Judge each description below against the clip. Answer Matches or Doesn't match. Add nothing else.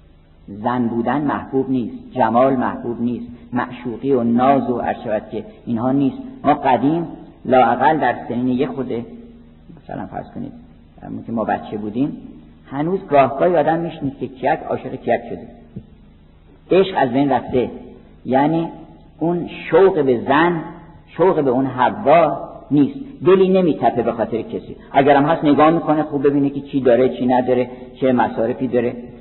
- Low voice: Matches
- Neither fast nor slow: Matches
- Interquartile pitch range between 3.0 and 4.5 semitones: Matches